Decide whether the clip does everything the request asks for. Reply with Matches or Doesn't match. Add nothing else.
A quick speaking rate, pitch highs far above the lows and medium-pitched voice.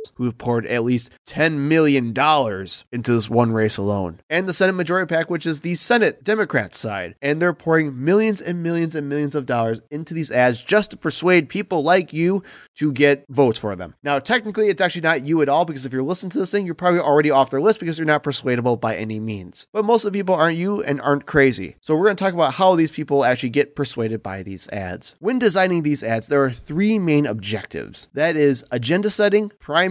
Matches